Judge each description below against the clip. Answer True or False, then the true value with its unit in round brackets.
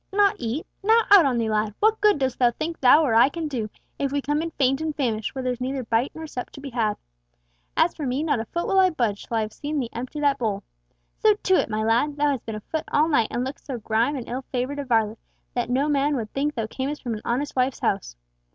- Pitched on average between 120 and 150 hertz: False (265 Hz)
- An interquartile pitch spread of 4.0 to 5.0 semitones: True (4.4 semitones)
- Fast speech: True (265 wpm)